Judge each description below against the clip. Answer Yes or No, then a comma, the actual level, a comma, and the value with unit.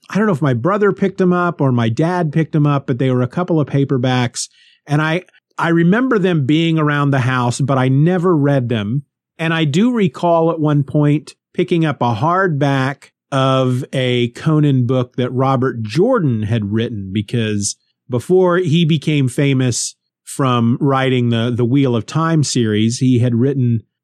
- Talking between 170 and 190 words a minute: Yes, average, 180 wpm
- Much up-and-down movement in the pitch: No, average, 4.6 semitones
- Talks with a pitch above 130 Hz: Yes, medium, 140 Hz